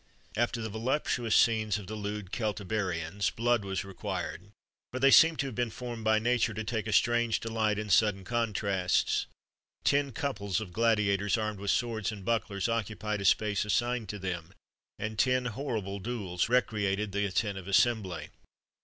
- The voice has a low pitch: Yes, low, 110 Hz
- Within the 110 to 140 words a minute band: No, average, 160 wpm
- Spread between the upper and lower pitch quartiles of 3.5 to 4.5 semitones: No, average, 2.8 semitones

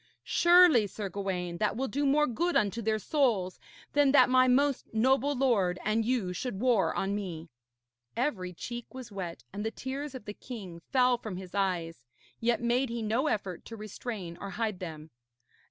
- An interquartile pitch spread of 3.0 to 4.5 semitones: No, average, 5.3 semitones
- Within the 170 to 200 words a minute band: Yes, average, 180 wpm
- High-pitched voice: Yes, high, 220 Hz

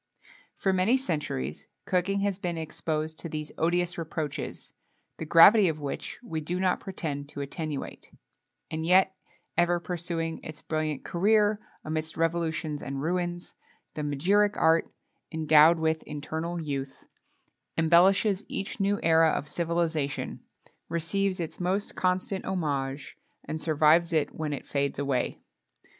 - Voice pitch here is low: No, medium, 165 Hz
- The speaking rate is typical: No, slow, 130 wpm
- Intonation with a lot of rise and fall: No, average, 2.9 semitones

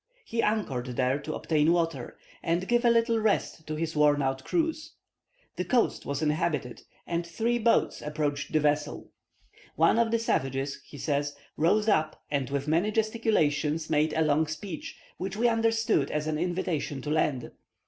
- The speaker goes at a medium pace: Yes, average, 170 wpm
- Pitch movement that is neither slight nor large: No, wide, 6.7 semitones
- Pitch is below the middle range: No, medium, 155 Hz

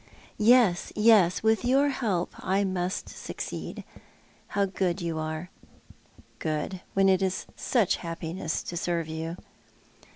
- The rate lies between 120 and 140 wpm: Yes, slow, 135 wpm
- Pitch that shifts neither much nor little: Yes, average, 3.4 semitones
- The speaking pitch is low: No, medium, 185 Hz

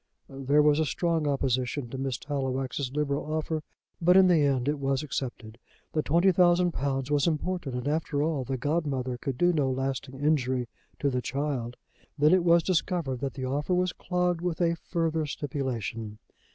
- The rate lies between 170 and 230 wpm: Yes, average, 180 wpm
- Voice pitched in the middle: Yes, medium, 145 Hz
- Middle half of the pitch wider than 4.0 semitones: No, average, 3.7 semitones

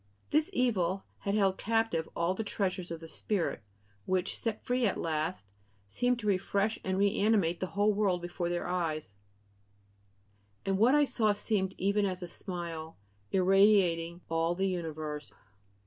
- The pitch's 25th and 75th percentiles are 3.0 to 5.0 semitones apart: Yes, average, 3.5 semitones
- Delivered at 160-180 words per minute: No, average, 150 wpm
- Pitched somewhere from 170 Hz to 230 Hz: Yes, high, 190 Hz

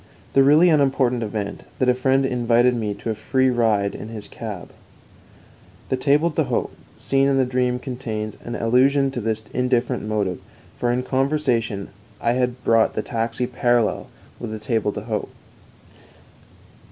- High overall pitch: No, low, 120 Hz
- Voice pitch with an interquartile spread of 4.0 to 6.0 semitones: No, average, 2.9 semitones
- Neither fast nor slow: Yes, average, 155 wpm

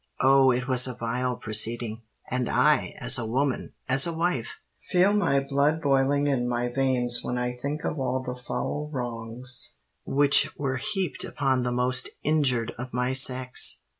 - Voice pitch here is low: Yes, low, 130 Hz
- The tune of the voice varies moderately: No, narrow, 2.1 semitones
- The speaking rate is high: No, average, 165 wpm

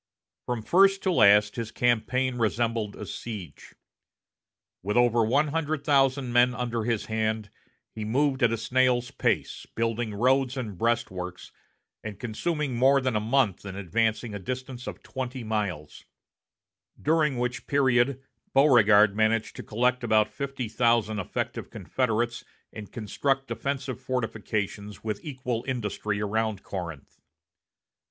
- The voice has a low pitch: Yes, low, 120 Hz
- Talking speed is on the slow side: Yes, slow, 130 wpm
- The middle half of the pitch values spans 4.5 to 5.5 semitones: No, average, 3.2 semitones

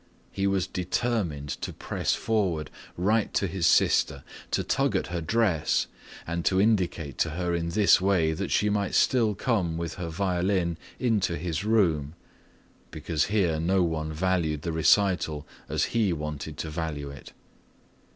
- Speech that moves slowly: No, average, 155 wpm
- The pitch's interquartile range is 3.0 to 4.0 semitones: Yes, average, 3.7 semitones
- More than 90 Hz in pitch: No, very low, 85 Hz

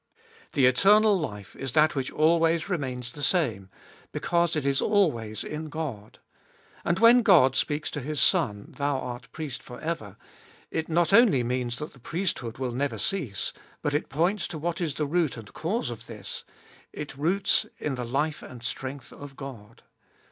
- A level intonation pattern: No, average, 5.2 semitones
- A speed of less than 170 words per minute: No, average, 175 wpm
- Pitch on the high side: No, medium, 145 Hz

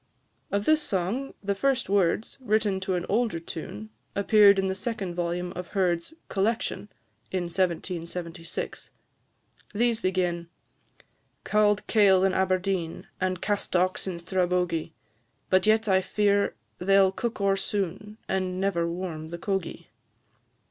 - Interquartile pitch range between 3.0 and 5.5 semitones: No, narrow, 2.5 semitones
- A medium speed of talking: No, slow, 130 wpm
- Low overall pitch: No, high, 190 Hz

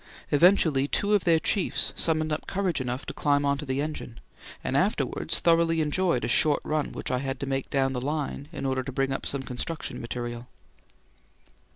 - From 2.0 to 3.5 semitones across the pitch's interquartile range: Yes, average, 3.2 semitones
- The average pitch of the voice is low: No, medium, 145 Hz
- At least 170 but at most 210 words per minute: Yes, average, 195 wpm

